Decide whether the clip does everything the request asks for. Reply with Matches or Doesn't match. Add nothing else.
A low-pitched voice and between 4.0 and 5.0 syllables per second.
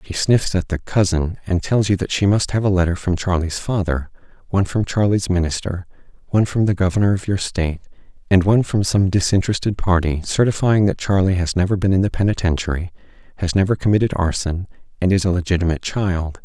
Doesn't match